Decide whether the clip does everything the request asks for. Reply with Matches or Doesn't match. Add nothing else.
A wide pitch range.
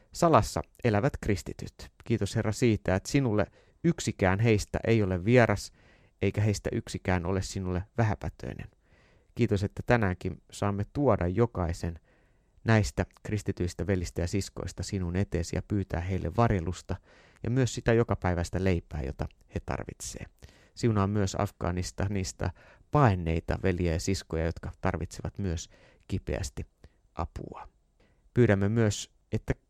Doesn't match